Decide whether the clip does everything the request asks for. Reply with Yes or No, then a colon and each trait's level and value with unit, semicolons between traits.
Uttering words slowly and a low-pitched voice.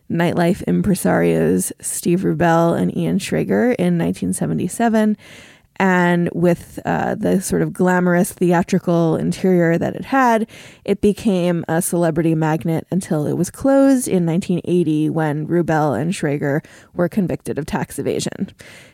No: slow, 130 wpm; medium, 175 Hz